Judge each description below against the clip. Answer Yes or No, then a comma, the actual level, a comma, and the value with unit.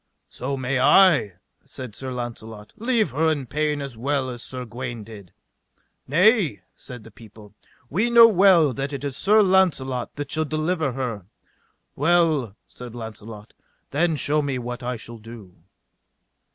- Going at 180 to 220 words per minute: No, average, 150 wpm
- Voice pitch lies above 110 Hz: Yes, low, 135 Hz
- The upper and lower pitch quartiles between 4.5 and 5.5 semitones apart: Yes, average, 5.1 semitones